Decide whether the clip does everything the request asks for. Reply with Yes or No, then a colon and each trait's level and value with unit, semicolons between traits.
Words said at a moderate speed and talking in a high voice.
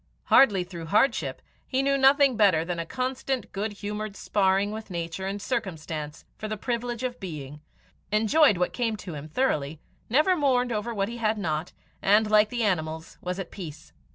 Yes: average, 180 wpm; high, 210 Hz